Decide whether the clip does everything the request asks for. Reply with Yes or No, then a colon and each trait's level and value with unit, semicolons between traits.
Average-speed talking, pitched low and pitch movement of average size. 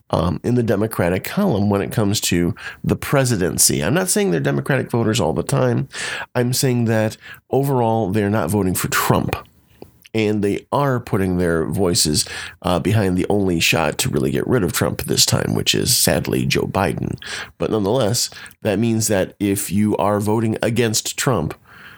Yes: average, 175 wpm; low, 105 Hz; average, 3.7 semitones